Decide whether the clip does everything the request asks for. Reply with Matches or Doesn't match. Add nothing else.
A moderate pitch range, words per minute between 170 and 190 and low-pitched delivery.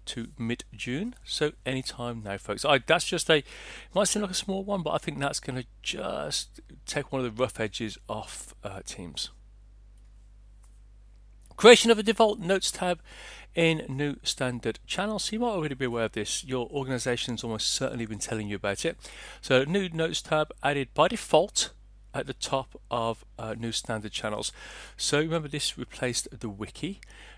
Doesn't match